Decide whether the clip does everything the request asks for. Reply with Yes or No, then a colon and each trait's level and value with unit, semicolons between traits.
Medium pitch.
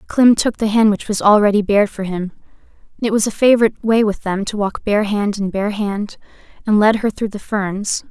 No: high, 210 Hz